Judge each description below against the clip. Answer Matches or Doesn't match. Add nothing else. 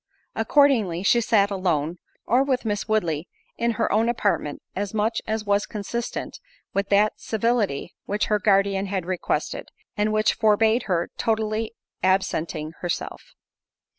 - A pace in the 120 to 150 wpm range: Matches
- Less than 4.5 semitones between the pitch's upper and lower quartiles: Matches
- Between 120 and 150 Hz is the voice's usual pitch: Doesn't match